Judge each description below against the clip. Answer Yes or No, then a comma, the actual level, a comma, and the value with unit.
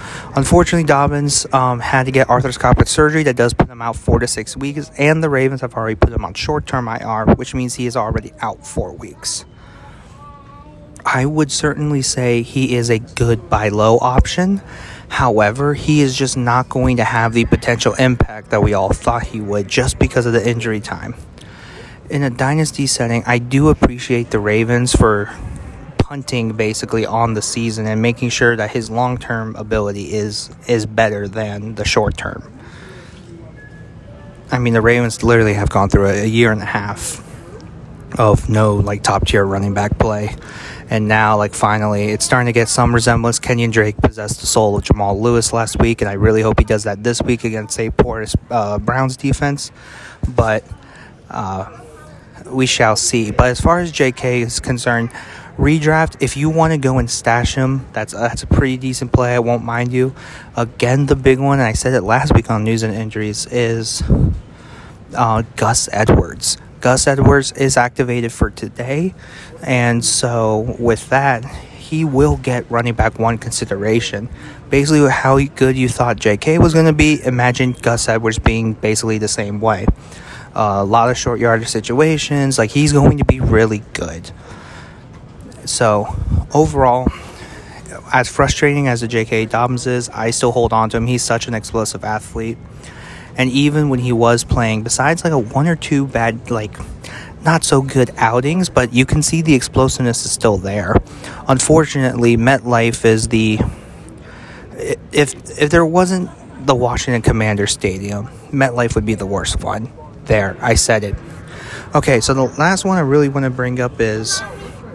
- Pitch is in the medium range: No, low, 120 Hz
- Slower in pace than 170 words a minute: No, average, 175 wpm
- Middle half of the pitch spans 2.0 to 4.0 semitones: Yes, average, 3.3 semitones